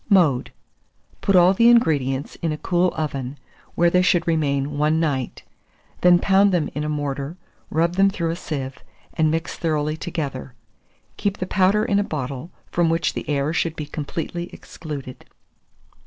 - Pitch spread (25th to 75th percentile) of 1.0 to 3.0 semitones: No, average, 3.6 semitones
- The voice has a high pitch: No, medium, 160 Hz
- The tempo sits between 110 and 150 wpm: No, average, 165 wpm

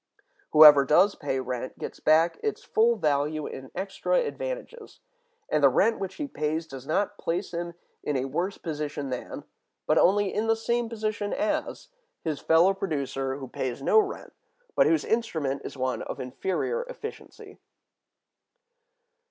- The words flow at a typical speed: Yes, average, 150 wpm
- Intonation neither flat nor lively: No, wide, 7.9 semitones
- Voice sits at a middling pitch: Yes, medium, 170 Hz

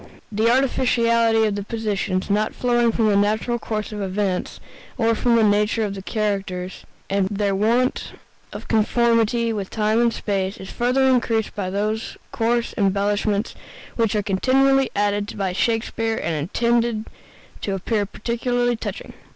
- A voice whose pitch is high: Yes, high, 215 Hz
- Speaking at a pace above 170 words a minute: No, average, 150 wpm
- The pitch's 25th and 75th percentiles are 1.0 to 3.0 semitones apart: Yes, narrow, 2.5 semitones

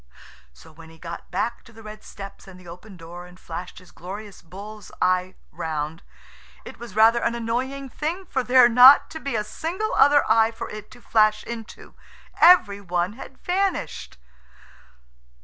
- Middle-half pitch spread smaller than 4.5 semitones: No, average, 5.3 semitones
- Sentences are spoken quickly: No, average, 170 wpm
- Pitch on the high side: Yes, high, 215 Hz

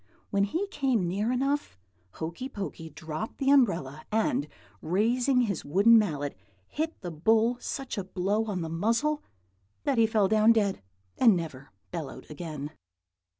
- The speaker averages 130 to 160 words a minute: Yes, average, 150 wpm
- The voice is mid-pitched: No, high, 210 Hz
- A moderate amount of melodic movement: No, wide, 6.8 semitones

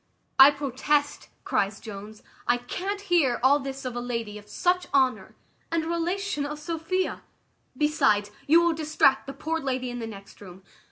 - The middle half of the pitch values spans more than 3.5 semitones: Yes, average, 5.2 semitones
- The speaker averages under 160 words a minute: No, average, 170 wpm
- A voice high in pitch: Yes, very high, 275 Hz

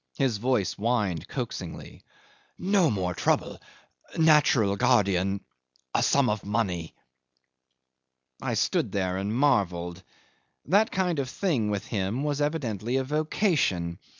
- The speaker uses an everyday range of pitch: No, wide, 7.4 semitones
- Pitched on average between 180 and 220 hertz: No, low, 110 Hz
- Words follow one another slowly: Yes, slow, 125 wpm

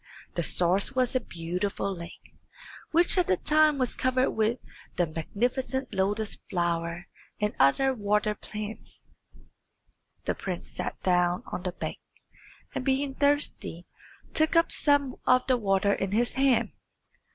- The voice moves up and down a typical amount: No, wide, 6.4 semitones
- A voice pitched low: No, high, 215 Hz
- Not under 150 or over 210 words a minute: No, average, 140 wpm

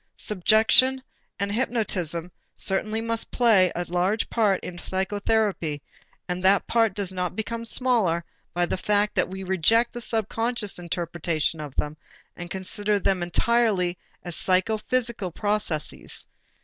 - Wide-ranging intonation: No, average, 4.0 semitones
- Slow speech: Yes, slow, 130 wpm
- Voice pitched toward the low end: No, high, 195 Hz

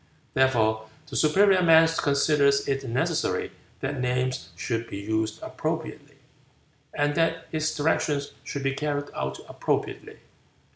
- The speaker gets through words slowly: Yes, slow, 125 wpm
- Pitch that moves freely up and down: No, average, 3.5 semitones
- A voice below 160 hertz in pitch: Yes, medium, 140 Hz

